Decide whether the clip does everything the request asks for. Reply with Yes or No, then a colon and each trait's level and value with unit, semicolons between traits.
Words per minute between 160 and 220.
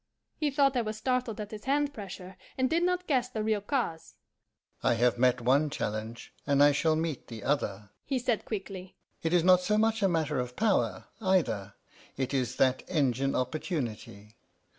Yes: average, 185 wpm